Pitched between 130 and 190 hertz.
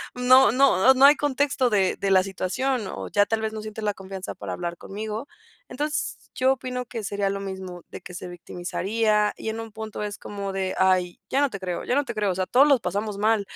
No: high, 210 Hz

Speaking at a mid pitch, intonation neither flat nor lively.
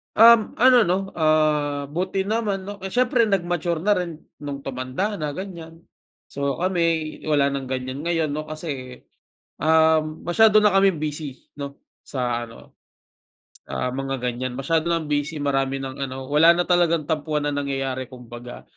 Yes: medium, 155 Hz; average, 4.4 semitones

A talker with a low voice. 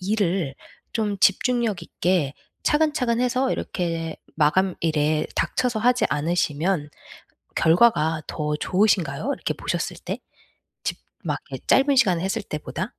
No: medium, 185 Hz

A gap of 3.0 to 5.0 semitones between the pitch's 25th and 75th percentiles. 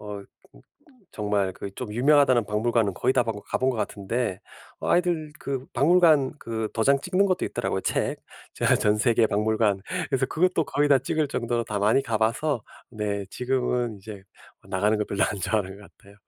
Yes: average, 4.7 semitones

